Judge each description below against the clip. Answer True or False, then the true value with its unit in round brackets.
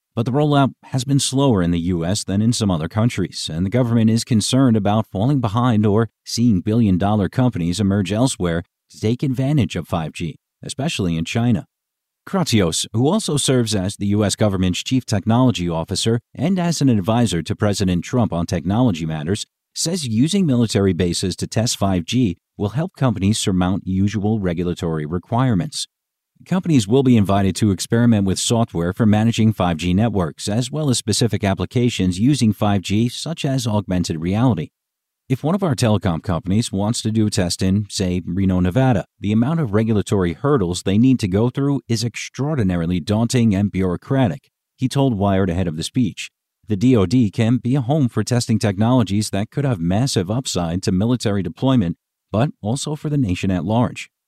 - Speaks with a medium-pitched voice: False (110 Hz)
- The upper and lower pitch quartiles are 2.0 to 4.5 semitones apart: False (5.1 semitones)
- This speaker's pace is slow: False (170 wpm)